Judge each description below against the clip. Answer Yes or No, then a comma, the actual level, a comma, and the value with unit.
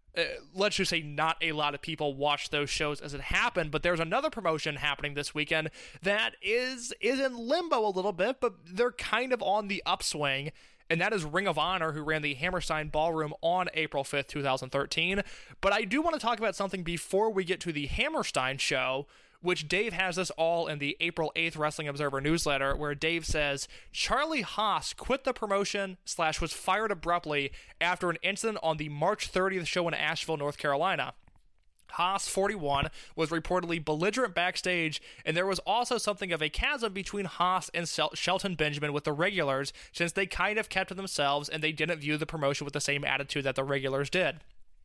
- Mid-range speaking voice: Yes, medium, 165 Hz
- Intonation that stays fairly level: No, average, 4.6 semitones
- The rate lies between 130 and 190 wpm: No, average, 200 wpm